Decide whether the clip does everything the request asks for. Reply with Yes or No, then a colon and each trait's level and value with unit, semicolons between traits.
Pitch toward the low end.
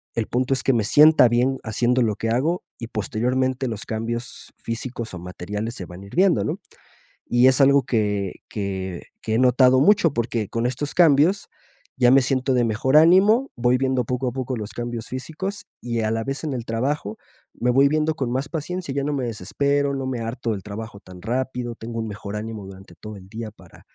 Yes: low, 120 Hz